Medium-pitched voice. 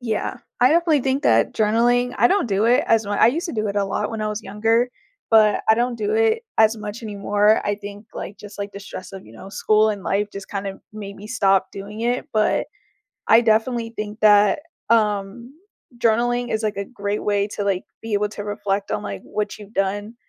No: high, 215 Hz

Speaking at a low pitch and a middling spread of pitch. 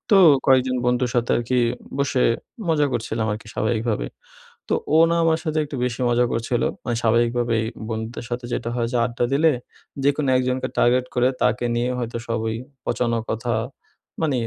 No: low, 120 Hz; narrow, 1.7 semitones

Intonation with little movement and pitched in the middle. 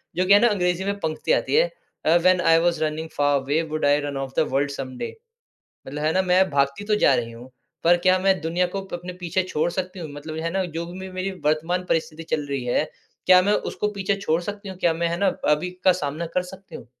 No: average, 3.6 semitones; medium, 170 Hz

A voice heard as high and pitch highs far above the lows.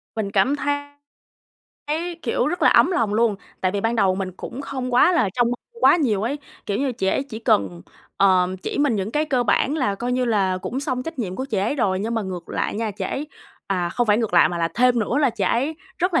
Yes: high, 230 Hz; wide, 5.7 semitones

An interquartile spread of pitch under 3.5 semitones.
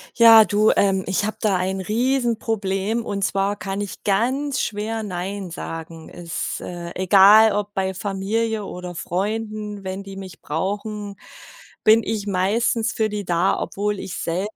Yes: narrow, 2.4 semitones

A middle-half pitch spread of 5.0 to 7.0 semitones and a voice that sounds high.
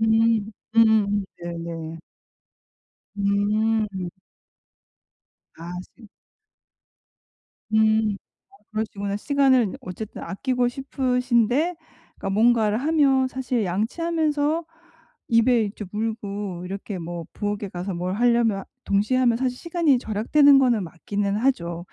No: average, 4.1 semitones; high, 220 Hz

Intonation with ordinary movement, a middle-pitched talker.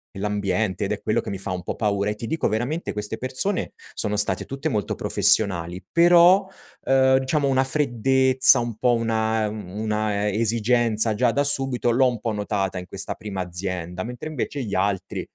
No: average, 4.5 semitones; low, 110 Hz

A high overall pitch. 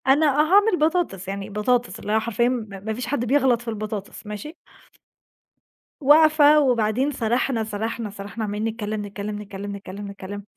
Yes: high, 220 Hz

